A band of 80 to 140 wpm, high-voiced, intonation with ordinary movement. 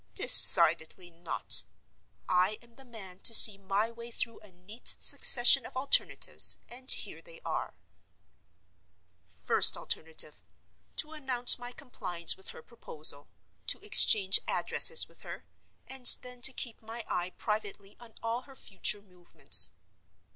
Yes: slow, 135 wpm; high, 225 Hz; average, 4.6 semitones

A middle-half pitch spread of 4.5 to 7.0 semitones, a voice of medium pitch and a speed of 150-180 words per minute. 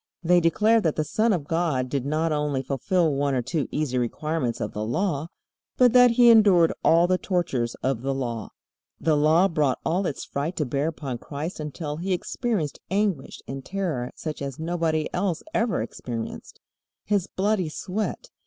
Yes: average, 5.1 semitones; medium, 160 Hz; average, 175 wpm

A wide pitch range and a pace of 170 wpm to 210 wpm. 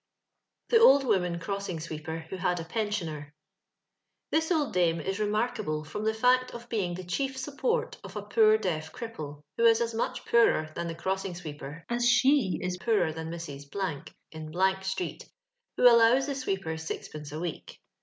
Yes: wide, 6.1 semitones; average, 175 wpm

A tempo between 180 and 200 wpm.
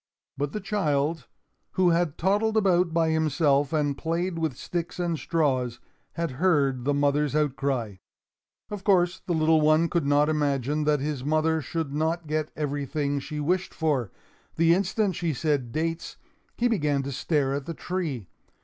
No: average, 160 wpm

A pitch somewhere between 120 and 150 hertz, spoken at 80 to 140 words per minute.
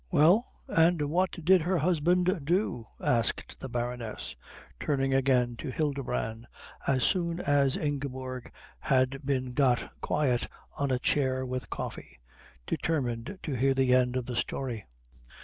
Yes: low, 135 Hz; slow, 135 wpm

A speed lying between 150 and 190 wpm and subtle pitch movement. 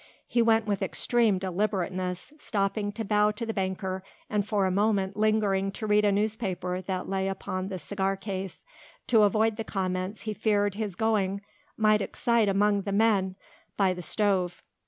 Yes: average, 170 wpm; narrow, 2.2 semitones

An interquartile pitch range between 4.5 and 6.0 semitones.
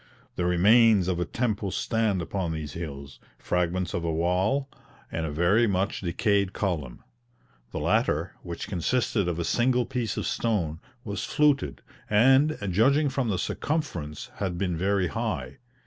Yes: average, 5.0 semitones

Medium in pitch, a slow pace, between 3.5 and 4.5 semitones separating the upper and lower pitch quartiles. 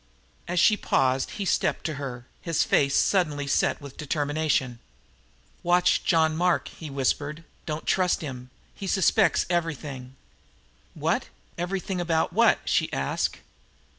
Yes: medium, 155 Hz; slow, 130 wpm; average, 4.1 semitones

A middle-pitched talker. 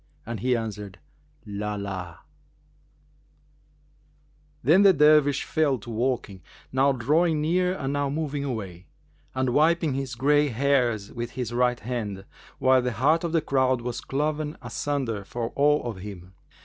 No: low, 130 Hz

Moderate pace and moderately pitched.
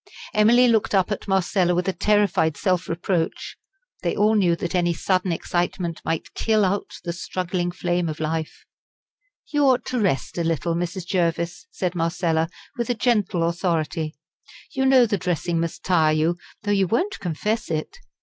Yes: average, 165 wpm; medium, 180 Hz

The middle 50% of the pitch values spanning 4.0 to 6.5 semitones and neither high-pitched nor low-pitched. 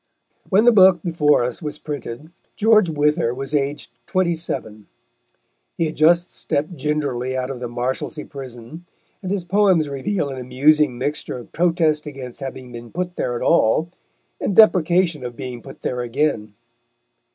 Yes: average, 5.3 semitones; medium, 150 Hz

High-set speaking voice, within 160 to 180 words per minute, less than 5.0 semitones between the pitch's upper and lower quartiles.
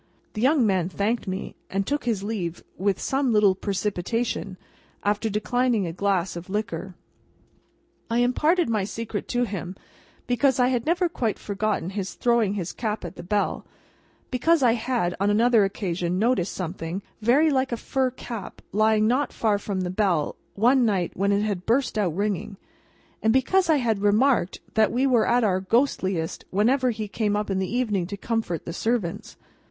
Yes: high, 215 Hz; average, 175 wpm; average, 4.0 semitones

